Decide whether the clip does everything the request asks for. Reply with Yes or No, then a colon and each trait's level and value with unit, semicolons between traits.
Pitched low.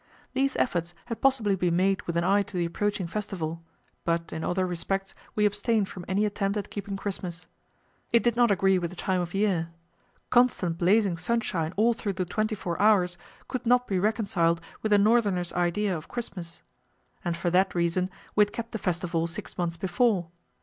No: high, 190 Hz